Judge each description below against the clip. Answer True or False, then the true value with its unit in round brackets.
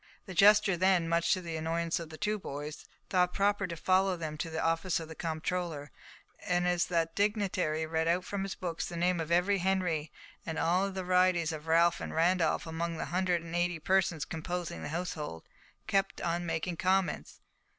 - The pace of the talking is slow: False (200 wpm)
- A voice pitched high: False (175 Hz)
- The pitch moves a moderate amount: False (2.3 semitones)